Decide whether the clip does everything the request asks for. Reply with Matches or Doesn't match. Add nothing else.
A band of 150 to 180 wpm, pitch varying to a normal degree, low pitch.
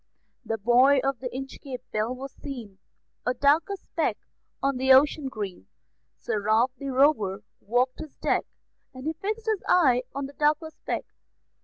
Doesn't match